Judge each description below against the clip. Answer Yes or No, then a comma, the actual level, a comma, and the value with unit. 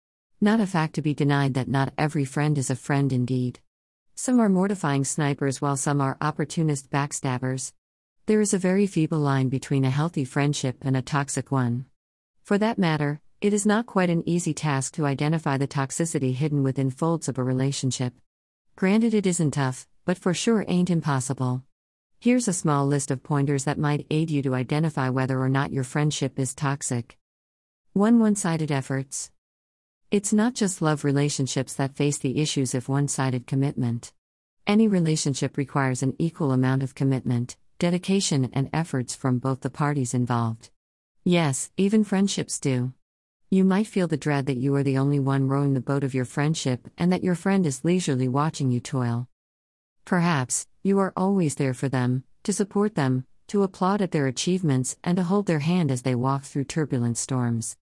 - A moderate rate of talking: Yes, average, 180 wpm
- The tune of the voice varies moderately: Yes, average, 4.2 semitones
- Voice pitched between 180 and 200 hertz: No, medium, 140 Hz